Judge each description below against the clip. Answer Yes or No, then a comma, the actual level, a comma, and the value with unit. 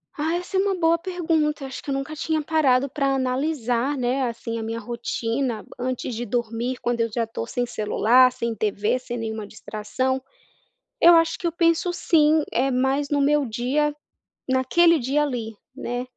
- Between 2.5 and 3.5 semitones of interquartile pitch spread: No, average, 4.2 semitones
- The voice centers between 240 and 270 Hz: Yes, very high, 260 Hz